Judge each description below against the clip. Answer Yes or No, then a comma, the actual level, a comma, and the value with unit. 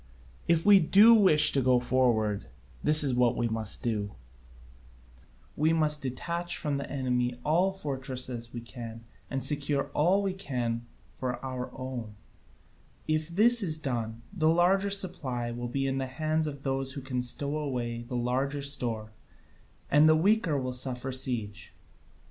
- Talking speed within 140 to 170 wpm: Yes, average, 160 wpm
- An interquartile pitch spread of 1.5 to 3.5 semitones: No, average, 4.2 semitones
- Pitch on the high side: No, low, 135 Hz